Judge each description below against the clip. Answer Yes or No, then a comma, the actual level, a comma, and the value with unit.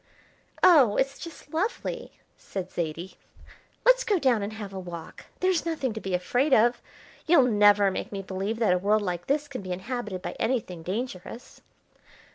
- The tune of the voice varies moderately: No, wide, 6.1 semitones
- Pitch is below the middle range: No, high, 215 Hz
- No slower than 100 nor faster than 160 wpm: No, average, 170 wpm